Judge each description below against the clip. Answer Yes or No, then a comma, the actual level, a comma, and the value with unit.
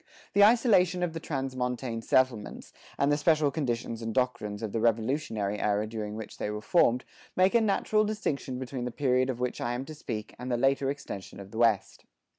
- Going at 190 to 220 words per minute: Yes, average, 200 wpm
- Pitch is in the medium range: No, low, 125 Hz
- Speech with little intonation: No, average, 4.6 semitones